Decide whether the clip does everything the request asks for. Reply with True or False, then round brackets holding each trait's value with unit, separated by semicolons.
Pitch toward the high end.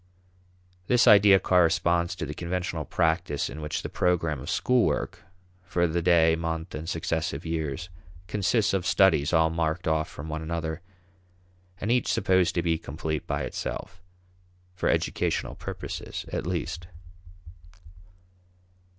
False (85 Hz)